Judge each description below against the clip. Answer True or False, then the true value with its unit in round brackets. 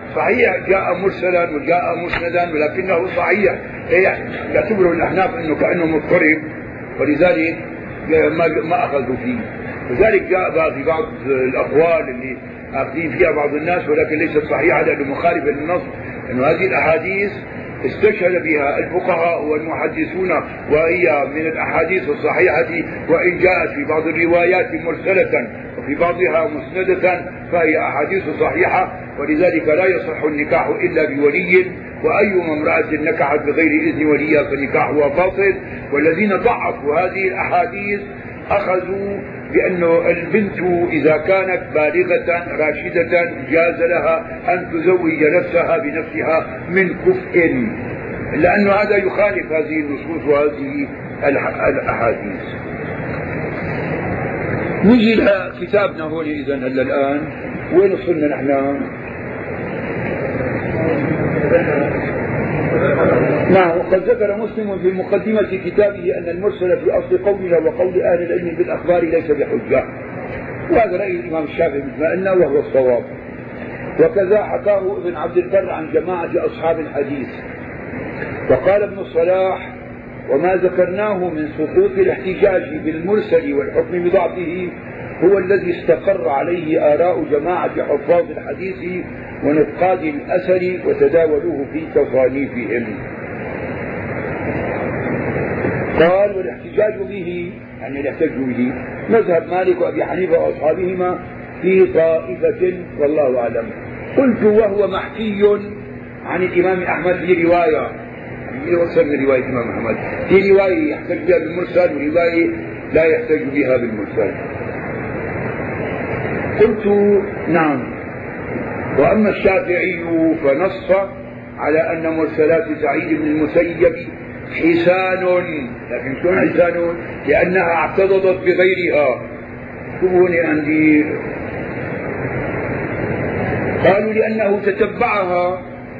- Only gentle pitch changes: False (3.9 semitones)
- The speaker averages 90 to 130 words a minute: True (100 wpm)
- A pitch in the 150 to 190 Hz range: True (175 Hz)